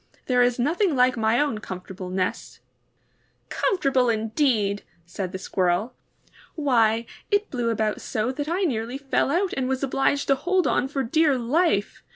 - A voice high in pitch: Yes, very high, 250 Hz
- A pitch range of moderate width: Yes, average, 4.7 semitones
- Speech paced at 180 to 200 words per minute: No, average, 160 wpm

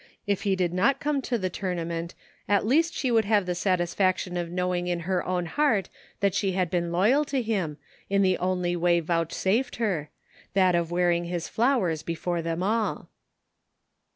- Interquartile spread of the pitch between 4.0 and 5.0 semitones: No, average, 3.2 semitones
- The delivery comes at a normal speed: Yes, average, 180 wpm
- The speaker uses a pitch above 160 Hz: Yes, medium, 185 Hz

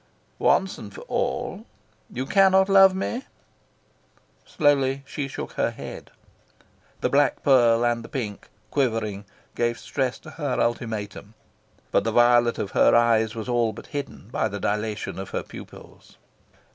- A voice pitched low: Yes, low, 120 Hz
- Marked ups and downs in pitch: No, average, 4.2 semitones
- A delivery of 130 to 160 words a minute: Yes, average, 145 wpm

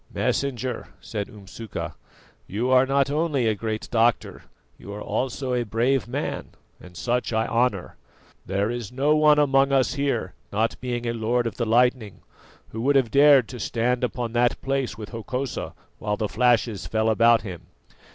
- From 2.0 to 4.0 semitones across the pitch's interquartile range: Yes, average, 3.1 semitones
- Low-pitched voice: Yes, low, 120 Hz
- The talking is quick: No, average, 170 wpm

